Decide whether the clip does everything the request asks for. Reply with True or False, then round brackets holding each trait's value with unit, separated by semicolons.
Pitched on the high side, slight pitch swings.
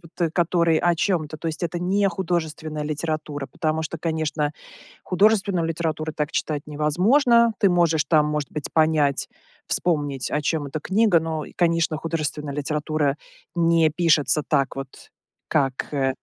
False (160 Hz; 2.2 semitones)